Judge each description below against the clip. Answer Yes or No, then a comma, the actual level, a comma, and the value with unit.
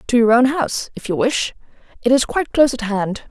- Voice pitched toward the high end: Yes, high, 245 Hz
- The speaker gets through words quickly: Yes, fast, 220 wpm